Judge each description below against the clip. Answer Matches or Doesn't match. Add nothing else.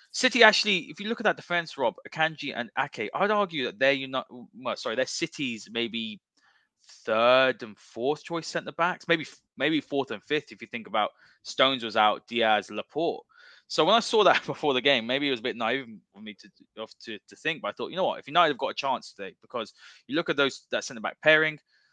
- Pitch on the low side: Doesn't match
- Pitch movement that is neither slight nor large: Doesn't match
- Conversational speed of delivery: Doesn't match